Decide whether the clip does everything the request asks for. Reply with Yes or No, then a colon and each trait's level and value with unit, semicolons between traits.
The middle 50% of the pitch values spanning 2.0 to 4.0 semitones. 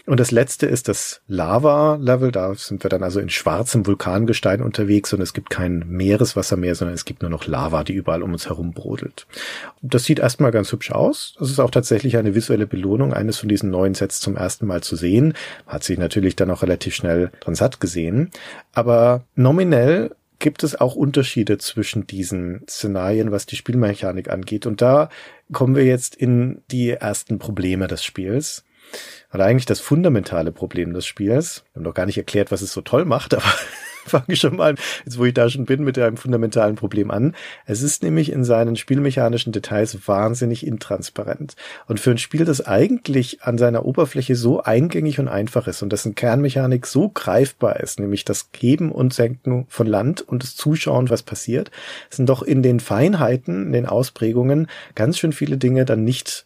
No: average, 4.8 semitones